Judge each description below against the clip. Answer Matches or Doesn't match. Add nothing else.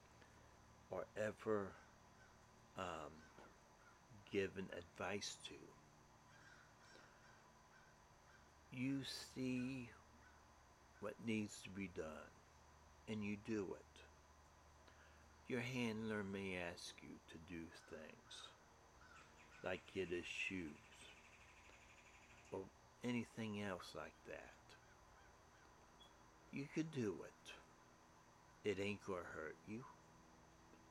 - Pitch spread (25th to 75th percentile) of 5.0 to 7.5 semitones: Matches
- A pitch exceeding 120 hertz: Doesn't match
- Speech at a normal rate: Doesn't match